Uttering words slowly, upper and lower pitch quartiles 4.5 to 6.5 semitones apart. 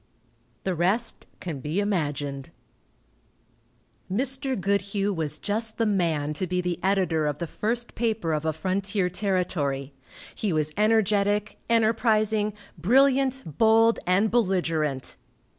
Yes: slow, 120 wpm; average, 5.3 semitones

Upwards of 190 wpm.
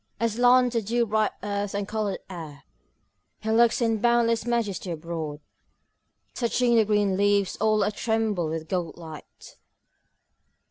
No: slow, 135 wpm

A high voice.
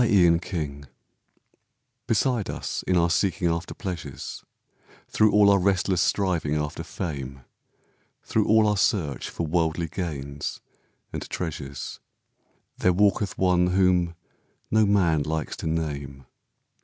No: very low, 85 Hz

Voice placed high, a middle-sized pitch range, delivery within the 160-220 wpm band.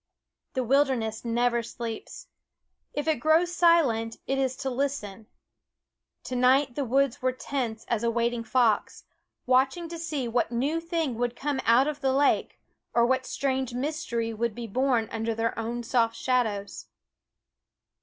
No: very high, 250 Hz; average, 3.2 semitones; average, 150 wpm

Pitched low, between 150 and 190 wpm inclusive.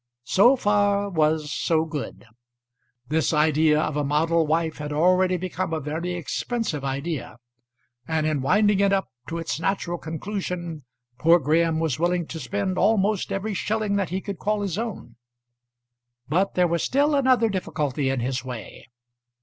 No: medium, 170 Hz; average, 160 wpm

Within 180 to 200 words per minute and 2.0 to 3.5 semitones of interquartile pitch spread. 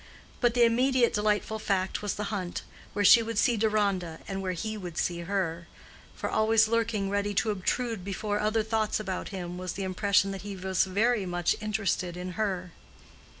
Yes: average, 185 wpm; average, 2.8 semitones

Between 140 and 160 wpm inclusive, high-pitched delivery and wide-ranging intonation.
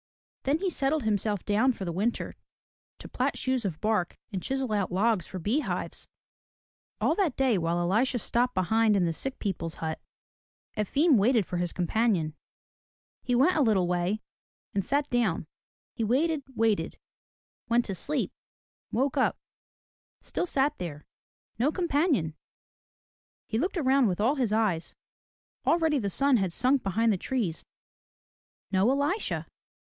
Yes: average, 155 wpm; high, 225 Hz; wide, 6.1 semitones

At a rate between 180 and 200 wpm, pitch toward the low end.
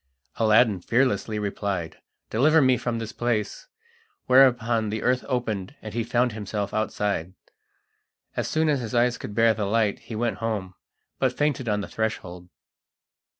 No: average, 150 wpm; low, 115 Hz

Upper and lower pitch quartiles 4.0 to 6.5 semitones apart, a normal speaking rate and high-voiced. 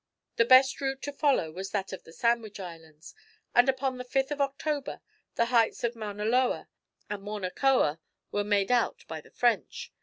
Yes: average, 5.2 semitones; average, 185 wpm; high, 235 Hz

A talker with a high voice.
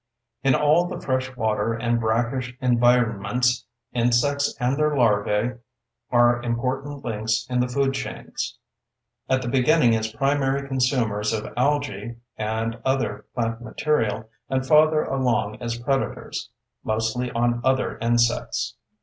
No: low, 125 Hz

